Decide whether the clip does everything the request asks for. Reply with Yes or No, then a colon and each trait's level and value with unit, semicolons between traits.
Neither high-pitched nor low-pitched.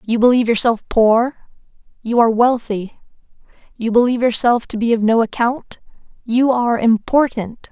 No: high, 235 Hz